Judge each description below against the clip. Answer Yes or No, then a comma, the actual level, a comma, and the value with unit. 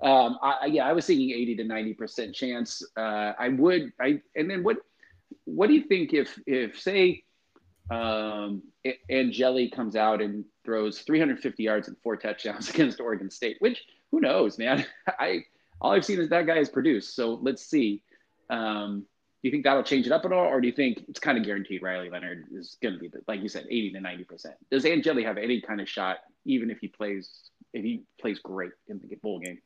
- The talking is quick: Yes, fast, 215 wpm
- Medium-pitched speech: No, low, 115 Hz